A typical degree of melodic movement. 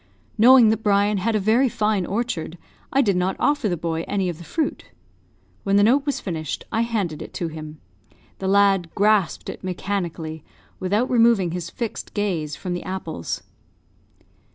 Yes: average, 4.3 semitones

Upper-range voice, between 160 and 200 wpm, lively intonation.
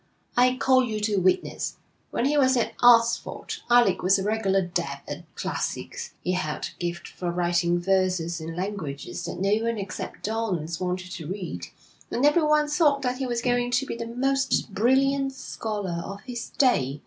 Yes: high, 210 Hz; average, 175 wpm; wide, 5.9 semitones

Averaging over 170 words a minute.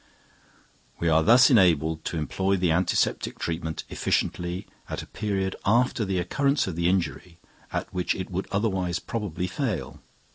No: average, 150 wpm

